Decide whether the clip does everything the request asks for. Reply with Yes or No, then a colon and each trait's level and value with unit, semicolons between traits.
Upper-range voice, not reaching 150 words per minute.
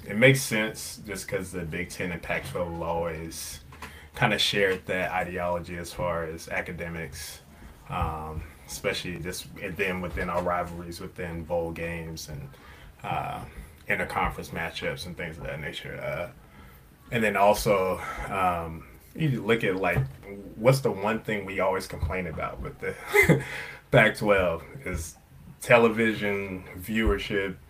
No: very low, 85 Hz; average, 140 wpm